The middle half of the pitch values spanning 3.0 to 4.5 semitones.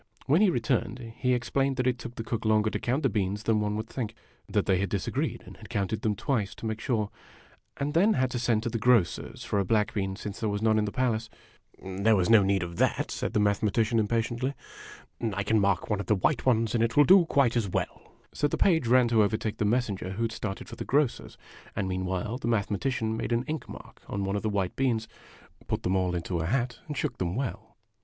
Yes: average, 3.4 semitones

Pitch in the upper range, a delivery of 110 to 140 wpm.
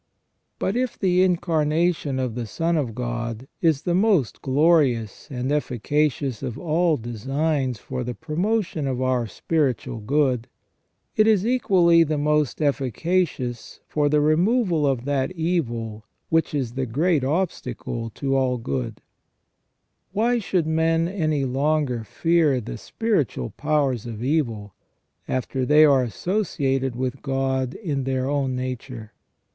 No: medium, 140 Hz; slow, 135 wpm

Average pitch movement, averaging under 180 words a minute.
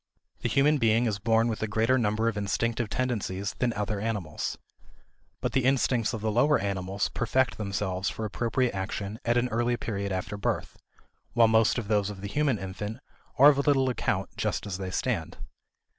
No: average, 3.3 semitones; average, 185 wpm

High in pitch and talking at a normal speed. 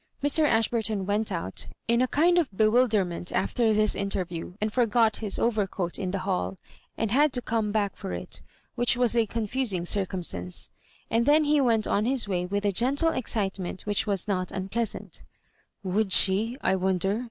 Yes: high, 210 Hz; average, 180 wpm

